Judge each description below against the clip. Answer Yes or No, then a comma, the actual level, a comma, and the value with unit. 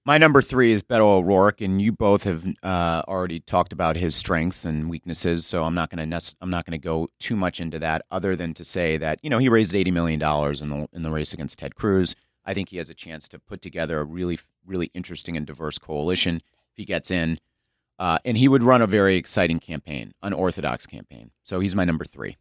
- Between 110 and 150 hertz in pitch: No, very low, 85 Hz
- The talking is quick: Yes, fast, 225 wpm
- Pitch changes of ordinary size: Yes, average, 3.2 semitones